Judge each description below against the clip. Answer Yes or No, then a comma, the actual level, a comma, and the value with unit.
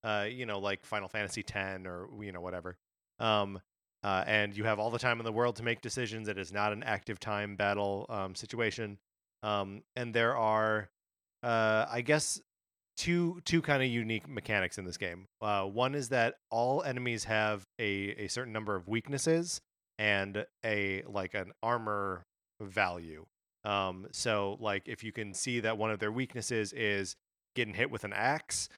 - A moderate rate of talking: Yes, average, 180 wpm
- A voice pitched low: Yes, low, 105 Hz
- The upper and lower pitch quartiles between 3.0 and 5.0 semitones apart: No, narrow, 2.6 semitones